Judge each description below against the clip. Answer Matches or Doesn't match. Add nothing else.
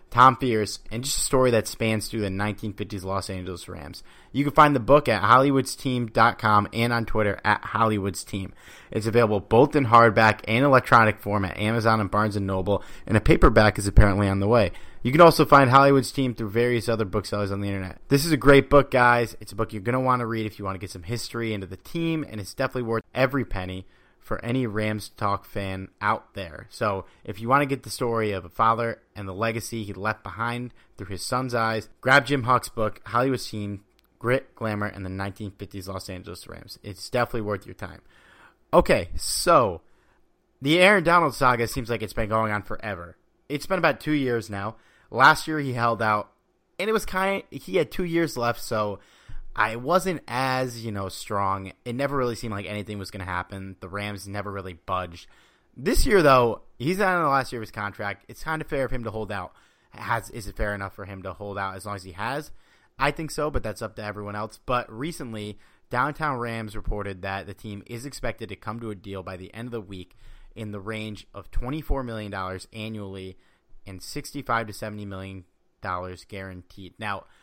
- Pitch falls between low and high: Doesn't match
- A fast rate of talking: Matches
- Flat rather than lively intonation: Doesn't match